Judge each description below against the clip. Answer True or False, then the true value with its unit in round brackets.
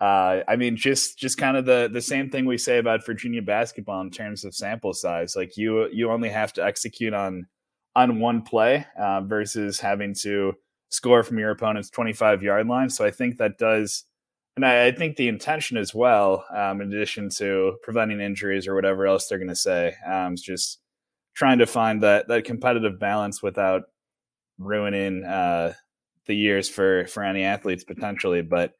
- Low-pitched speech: True (105 Hz)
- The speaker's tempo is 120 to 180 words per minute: False (190 wpm)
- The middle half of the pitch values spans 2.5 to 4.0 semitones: True (3.3 semitones)